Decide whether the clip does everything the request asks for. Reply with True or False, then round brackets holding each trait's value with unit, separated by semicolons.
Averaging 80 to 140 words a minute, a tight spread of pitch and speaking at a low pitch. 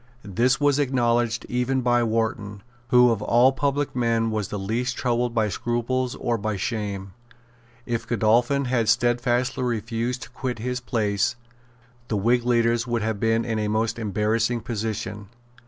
False (155 wpm; 2.1 semitones; 115 Hz)